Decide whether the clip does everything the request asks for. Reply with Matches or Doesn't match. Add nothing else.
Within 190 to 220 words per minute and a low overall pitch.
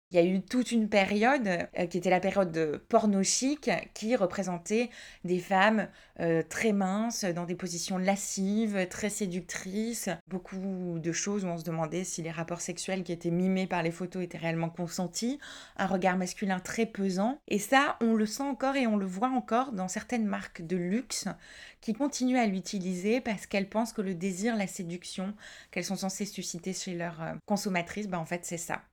Doesn't match